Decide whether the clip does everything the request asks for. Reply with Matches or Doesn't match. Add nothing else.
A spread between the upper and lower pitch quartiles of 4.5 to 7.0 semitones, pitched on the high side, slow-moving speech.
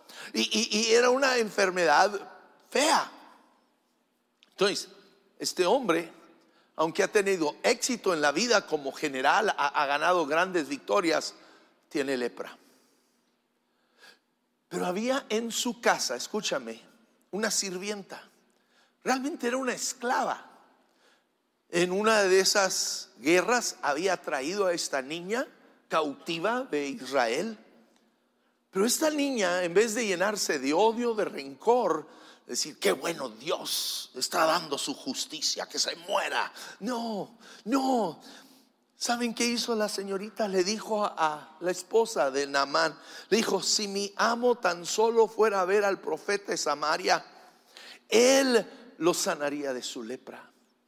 Matches